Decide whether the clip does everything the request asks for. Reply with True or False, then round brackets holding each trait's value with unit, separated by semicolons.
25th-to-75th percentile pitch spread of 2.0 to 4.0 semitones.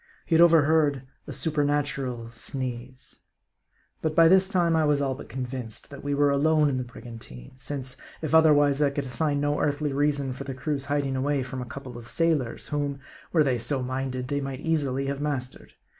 True (2.4 semitones)